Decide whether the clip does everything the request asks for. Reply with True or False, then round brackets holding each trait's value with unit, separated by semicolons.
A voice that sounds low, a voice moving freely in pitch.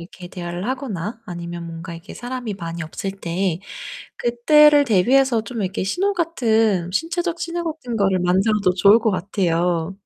False (200 Hz; 6.2 semitones)